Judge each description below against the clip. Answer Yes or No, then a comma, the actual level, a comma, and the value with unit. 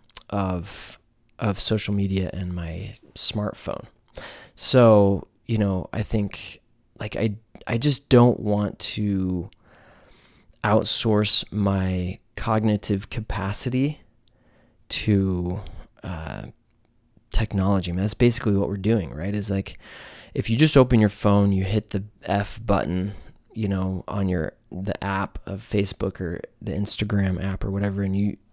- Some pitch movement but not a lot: No, narrow, 2.2 semitones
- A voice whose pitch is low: Yes, low, 100 Hz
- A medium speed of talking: No, slow, 130 wpm